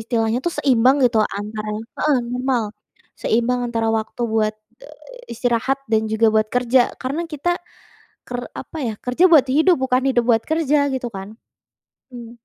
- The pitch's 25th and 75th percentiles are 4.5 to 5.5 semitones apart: No, average, 3.2 semitones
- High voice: Yes, high, 245 Hz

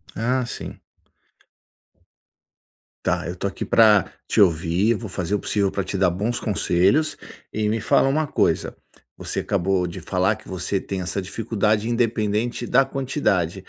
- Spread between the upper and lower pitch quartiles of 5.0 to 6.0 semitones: No, average, 3.8 semitones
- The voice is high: No, low, 105 Hz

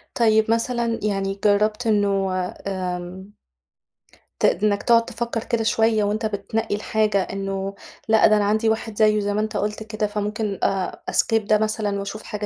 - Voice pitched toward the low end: No, high, 210 Hz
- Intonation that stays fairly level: Yes, narrow, 1.6 semitones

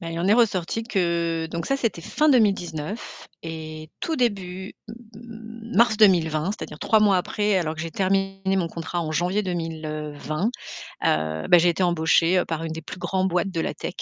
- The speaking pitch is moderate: Yes, medium, 180 Hz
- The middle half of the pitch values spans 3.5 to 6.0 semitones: Yes, average, 4.1 semitones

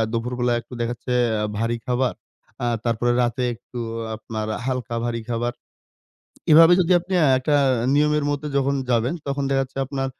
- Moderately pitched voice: No, low, 125 Hz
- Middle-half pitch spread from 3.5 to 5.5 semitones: No, average, 3.0 semitones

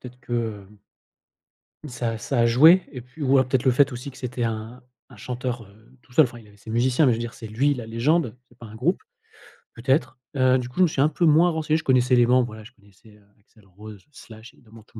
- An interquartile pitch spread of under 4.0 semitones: Yes, average, 2.9 semitones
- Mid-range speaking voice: No, low, 125 Hz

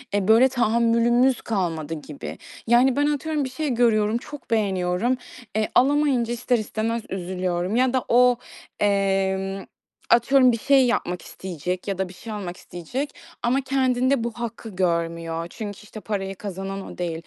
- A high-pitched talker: Yes, high, 220 Hz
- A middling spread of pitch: Yes, average, 4.8 semitones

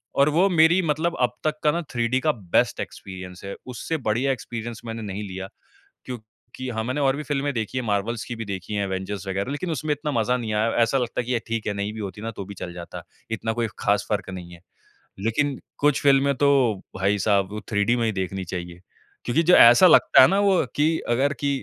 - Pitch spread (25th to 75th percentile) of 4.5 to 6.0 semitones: Yes, wide, 5.6 semitones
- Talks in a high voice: No, low, 115 Hz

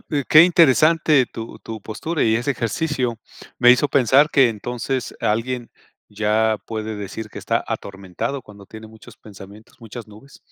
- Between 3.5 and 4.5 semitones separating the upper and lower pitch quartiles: Yes, average, 3.9 semitones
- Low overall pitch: Yes, low, 115 Hz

